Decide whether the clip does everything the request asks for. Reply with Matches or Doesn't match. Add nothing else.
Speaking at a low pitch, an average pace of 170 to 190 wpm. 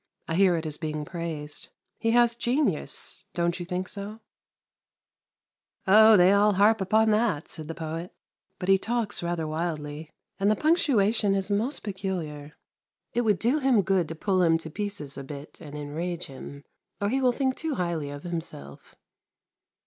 Doesn't match